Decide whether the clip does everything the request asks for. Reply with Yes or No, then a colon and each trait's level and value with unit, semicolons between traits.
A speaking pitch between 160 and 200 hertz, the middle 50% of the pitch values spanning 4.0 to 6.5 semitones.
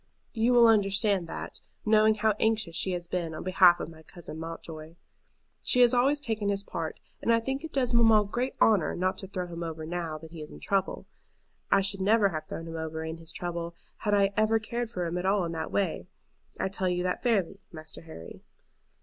Yes: high, 190 Hz; average, 4.7 semitones